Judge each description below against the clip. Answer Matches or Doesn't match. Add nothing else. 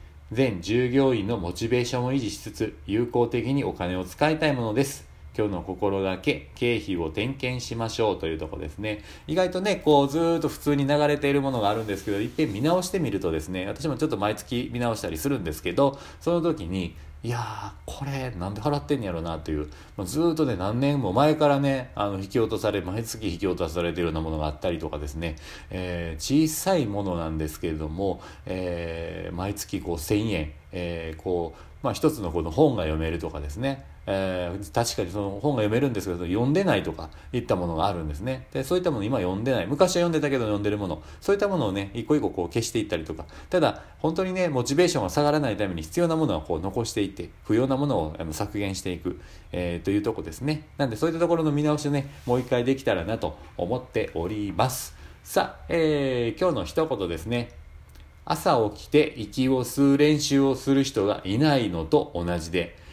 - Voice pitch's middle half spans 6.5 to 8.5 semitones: Matches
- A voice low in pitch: Matches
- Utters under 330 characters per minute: Doesn't match